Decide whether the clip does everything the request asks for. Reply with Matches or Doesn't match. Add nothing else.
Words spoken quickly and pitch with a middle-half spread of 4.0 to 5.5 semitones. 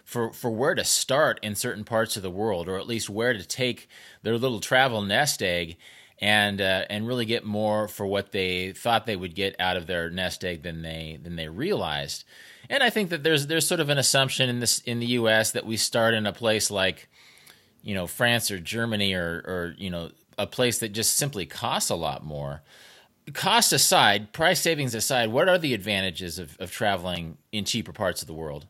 Matches